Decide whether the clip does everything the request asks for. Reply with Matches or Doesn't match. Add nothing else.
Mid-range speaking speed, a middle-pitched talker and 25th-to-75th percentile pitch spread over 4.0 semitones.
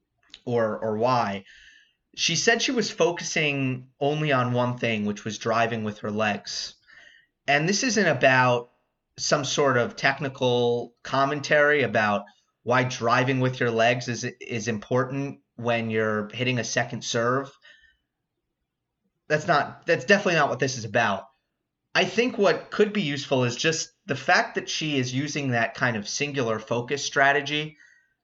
Doesn't match